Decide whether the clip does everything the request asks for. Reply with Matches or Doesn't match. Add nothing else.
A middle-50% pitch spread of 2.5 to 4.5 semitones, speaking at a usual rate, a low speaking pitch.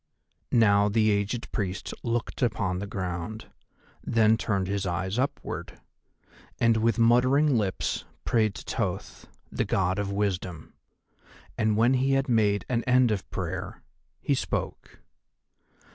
Doesn't match